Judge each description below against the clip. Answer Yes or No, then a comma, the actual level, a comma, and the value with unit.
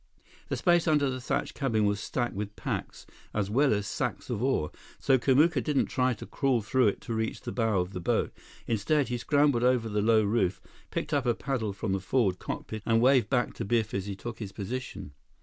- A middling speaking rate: No, fast, 220 wpm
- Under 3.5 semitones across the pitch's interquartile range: No, average, 4.2 semitones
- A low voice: Yes, low, 115 Hz